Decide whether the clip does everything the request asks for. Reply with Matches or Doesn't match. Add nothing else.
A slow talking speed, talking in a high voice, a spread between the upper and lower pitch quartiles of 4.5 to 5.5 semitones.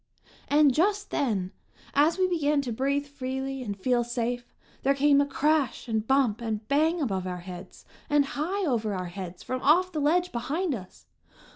Doesn't match